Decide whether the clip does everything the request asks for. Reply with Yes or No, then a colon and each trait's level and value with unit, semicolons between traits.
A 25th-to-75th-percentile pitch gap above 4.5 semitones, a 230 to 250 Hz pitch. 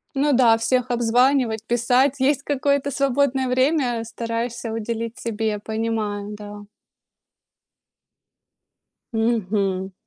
No: average, 2.9 semitones; high, 235 Hz